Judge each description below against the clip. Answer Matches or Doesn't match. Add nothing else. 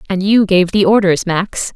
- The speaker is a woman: Matches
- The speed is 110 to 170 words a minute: Doesn't match